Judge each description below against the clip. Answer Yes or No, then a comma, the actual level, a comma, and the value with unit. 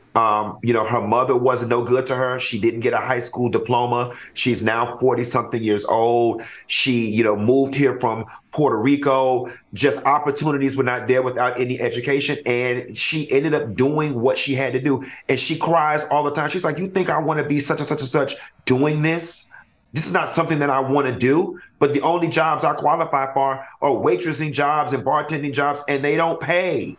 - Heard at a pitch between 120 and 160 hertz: Yes, low, 135 Hz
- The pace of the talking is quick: Yes, fast, 215 wpm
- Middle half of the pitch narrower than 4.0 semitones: Yes, average, 3.4 semitones